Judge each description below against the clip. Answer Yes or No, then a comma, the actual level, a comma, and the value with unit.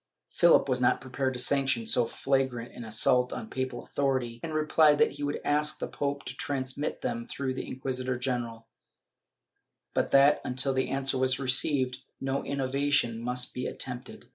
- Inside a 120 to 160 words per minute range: No, average, 175 wpm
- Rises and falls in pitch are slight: Yes, narrow, 1.9 semitones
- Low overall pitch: Yes, low, 130 Hz